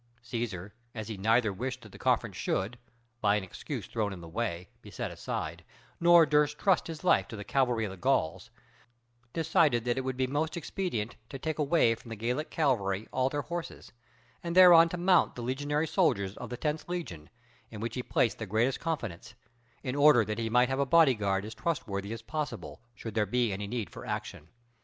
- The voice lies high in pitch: No, low, 120 Hz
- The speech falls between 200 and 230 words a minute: Yes, fast, 205 wpm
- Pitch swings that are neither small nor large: No, wide, 6.0 semitones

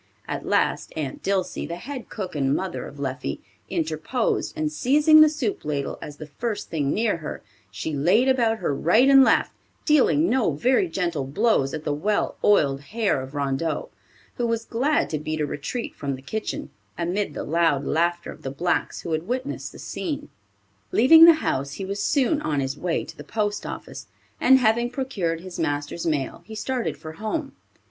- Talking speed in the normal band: Yes, average, 185 wpm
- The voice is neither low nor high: Yes, medium, 180 Hz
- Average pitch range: No, wide, 8.4 semitones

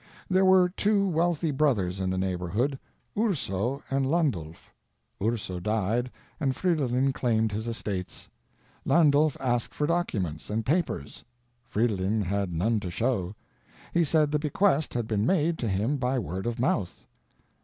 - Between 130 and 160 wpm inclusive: Yes, average, 145 wpm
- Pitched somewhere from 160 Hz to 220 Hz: No, low, 120 Hz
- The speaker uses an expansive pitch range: Yes, wide, 7.1 semitones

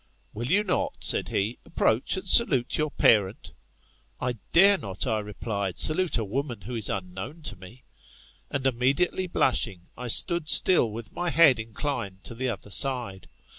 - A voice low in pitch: Yes, low, 120 Hz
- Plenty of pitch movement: Yes, wide, 6.8 semitones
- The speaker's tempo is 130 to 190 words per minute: Yes, average, 170 wpm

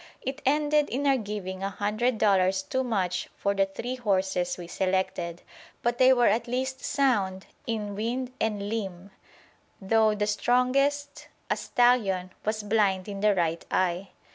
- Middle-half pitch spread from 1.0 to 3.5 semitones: No, average, 4.6 semitones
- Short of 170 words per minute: Yes, average, 155 wpm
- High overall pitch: Yes, high, 210 Hz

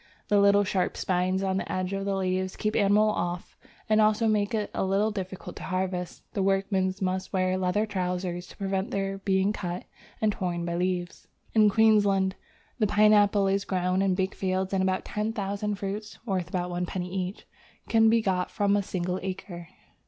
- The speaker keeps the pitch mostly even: Yes, narrow, 1.9 semitones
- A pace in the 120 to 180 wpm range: No, average, 190 wpm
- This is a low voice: No, high, 195 Hz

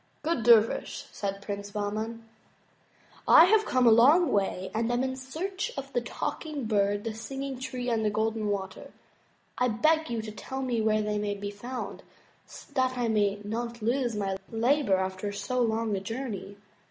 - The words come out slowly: No, average, 175 wpm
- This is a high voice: Yes, high, 225 Hz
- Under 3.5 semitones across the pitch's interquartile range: No, average, 3.9 semitones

